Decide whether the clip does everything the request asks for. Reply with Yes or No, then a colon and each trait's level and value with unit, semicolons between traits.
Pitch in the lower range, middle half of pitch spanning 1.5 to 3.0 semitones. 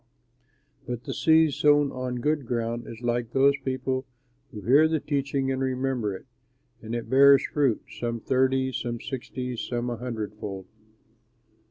Yes: low, 130 Hz; narrow, 2.5 semitones